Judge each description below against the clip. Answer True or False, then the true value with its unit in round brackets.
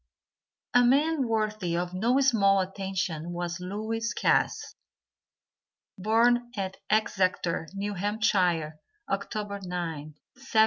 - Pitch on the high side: True (200 Hz)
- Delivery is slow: True (100 wpm)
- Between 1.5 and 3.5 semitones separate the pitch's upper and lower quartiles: False (4.0 semitones)